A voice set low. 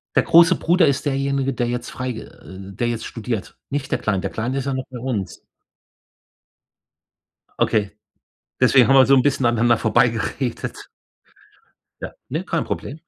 Yes: low, 125 Hz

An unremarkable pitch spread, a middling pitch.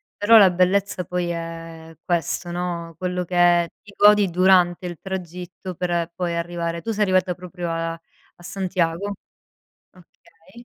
No: narrow, 1.7 semitones; medium, 175 Hz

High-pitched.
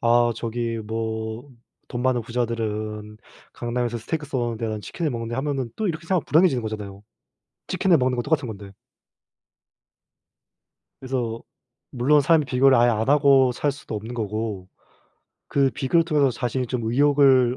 No: low, 120 Hz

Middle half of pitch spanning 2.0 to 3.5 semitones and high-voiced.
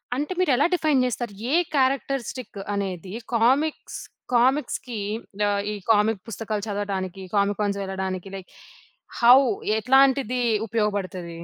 No: average, 4.7 semitones; high, 220 Hz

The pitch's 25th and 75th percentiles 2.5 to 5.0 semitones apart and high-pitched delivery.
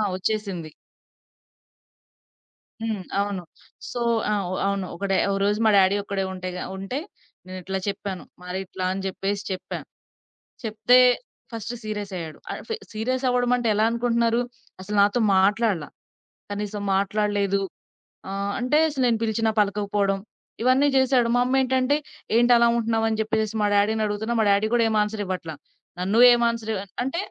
Yes: average, 3.0 semitones; high, 210 Hz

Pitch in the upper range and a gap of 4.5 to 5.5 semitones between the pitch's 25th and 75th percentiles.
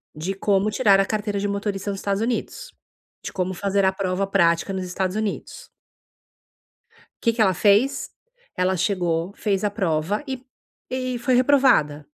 No: high, 200 Hz; average, 2.7 semitones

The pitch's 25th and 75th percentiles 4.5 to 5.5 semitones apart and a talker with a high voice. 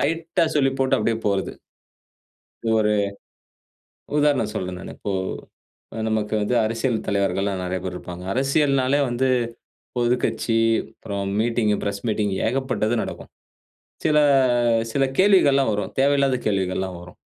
No: average, 5.2 semitones; low, 115 Hz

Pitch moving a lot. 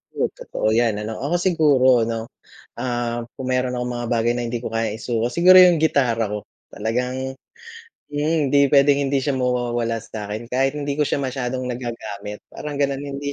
No: average, 3.3 semitones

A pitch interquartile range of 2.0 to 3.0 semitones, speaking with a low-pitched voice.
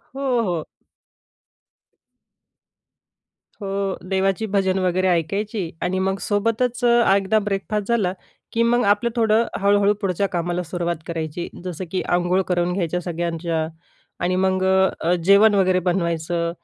No: narrow, 2.6 semitones; high, 190 Hz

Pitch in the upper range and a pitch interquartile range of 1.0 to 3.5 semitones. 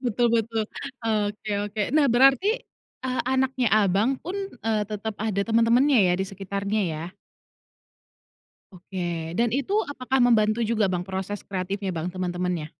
No: high, 215 Hz; average, 4.1 semitones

